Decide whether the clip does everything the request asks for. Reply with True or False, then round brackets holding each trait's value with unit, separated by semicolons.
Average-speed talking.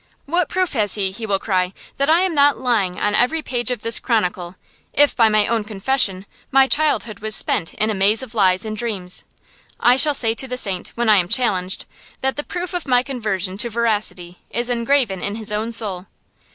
False (210 wpm)